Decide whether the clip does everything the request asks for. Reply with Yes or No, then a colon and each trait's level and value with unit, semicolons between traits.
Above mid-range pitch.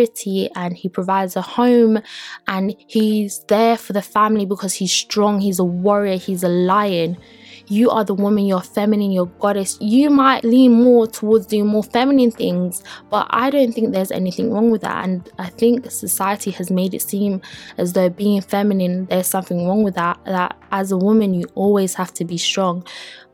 Yes: high, 200 Hz